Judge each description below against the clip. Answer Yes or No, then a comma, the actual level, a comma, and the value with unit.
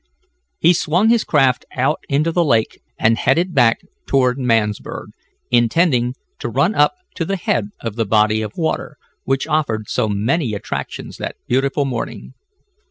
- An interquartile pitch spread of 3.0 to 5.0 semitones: No, wide, 5.5 semitones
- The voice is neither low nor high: No, low, 130 Hz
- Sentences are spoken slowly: No, average, 155 wpm